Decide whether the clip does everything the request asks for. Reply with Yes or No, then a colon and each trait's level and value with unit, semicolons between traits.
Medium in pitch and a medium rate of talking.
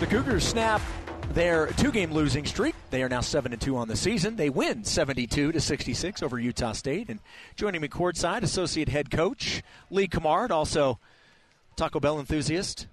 Yes: medium, 150 Hz; average, 160 wpm